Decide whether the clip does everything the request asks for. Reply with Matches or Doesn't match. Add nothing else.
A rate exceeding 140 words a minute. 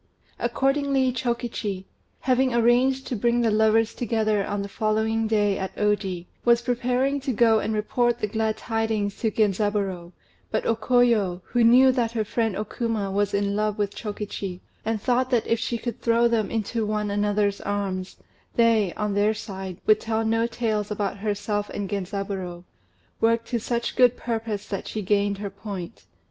Matches